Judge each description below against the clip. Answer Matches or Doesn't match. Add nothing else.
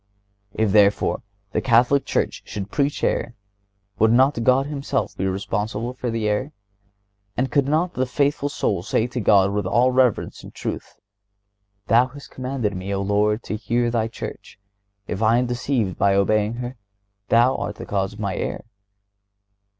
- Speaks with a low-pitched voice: Matches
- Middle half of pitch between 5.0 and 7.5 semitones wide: Doesn't match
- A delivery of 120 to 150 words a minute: Doesn't match